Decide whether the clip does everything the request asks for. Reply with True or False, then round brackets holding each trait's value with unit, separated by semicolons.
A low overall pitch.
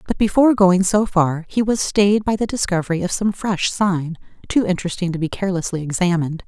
False (185 Hz)